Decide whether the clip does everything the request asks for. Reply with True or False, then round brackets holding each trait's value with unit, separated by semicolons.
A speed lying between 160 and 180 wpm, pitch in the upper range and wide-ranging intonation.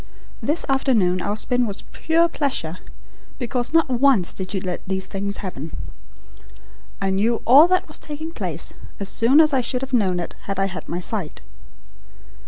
True (175 wpm; 225 Hz; 6.1 semitones)